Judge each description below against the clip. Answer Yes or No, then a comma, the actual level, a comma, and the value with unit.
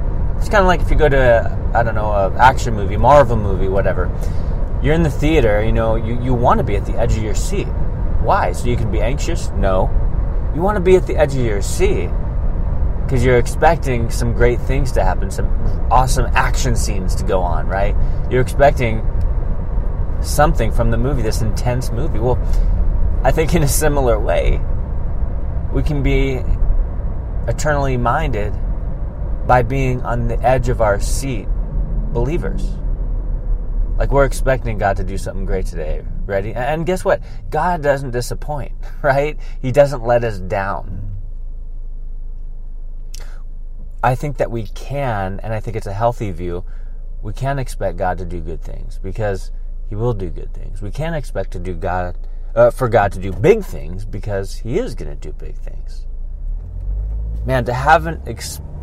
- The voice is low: Yes, low, 105 Hz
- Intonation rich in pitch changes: Yes, wide, 5.7 semitones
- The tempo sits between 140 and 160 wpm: No, average, 175 wpm